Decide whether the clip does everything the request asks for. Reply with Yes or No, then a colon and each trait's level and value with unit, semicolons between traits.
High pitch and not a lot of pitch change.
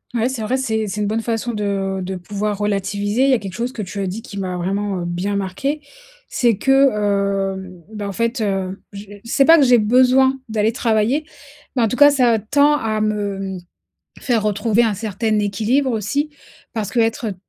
No: high, 215 Hz; average, 3.2 semitones